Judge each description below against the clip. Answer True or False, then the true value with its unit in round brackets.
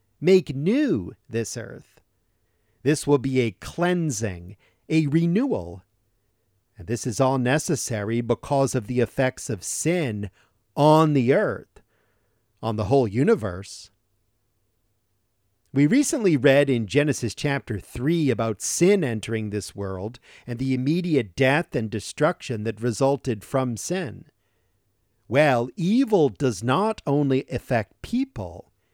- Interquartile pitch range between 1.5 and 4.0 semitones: False (5.2 semitones)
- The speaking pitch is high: False (120 Hz)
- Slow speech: True (120 wpm)